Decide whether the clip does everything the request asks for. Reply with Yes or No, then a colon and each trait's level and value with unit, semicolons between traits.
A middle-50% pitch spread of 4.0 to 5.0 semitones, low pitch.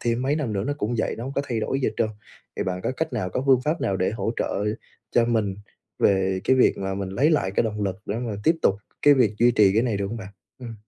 Yes: average, 4.5 semitones; low, 115 Hz